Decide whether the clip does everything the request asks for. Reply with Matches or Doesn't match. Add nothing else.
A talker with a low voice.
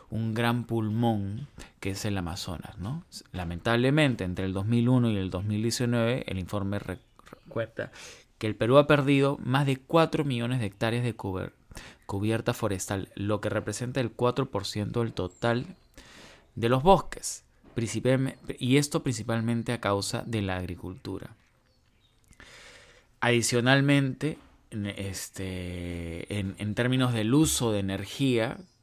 Matches